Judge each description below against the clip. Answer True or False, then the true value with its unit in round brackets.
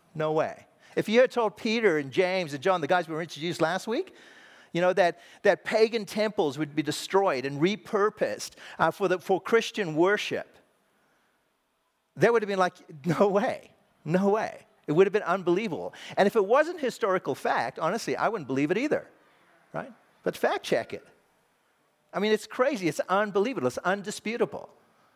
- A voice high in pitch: True (195 Hz)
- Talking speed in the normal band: True (175 wpm)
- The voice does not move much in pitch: False (4.0 semitones)